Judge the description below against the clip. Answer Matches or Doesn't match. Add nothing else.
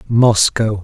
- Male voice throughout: Matches